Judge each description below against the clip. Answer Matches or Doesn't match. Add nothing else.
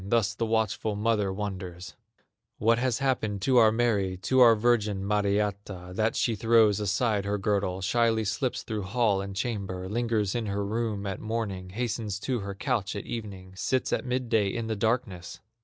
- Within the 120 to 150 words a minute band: Doesn't match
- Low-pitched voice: Matches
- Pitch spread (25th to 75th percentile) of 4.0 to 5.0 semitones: Doesn't match